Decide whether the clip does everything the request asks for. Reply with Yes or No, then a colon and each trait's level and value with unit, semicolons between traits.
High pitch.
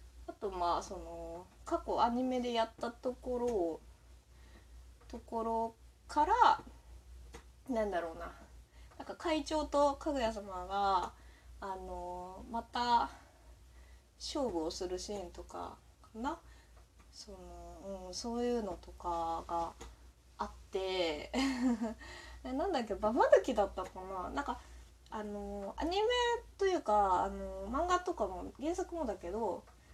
Yes: high, 210 Hz